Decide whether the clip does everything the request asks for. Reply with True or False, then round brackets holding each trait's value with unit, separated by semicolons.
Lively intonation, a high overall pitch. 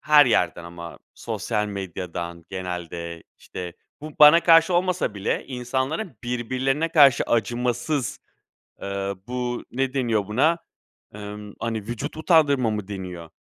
False (6.3 semitones; 120 Hz)